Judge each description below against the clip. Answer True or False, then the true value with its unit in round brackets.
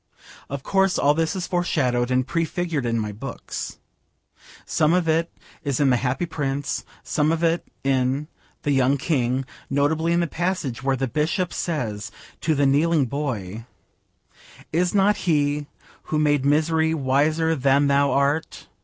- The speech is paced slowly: False (155 wpm)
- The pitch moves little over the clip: False (3.5 semitones)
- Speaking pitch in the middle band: True (145 Hz)